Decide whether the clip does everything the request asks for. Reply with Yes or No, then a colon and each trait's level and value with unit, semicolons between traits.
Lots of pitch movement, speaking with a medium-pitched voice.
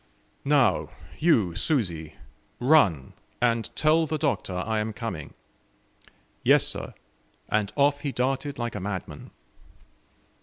No: wide, 6.7 semitones; low, 120 Hz